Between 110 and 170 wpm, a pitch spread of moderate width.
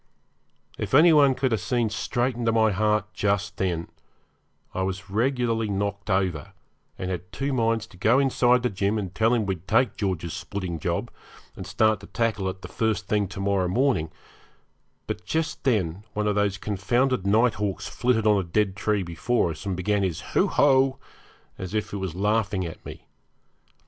No: average, 180 wpm; average, 3.4 semitones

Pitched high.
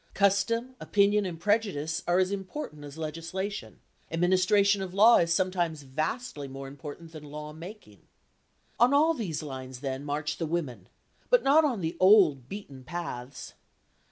No: medium, 170 Hz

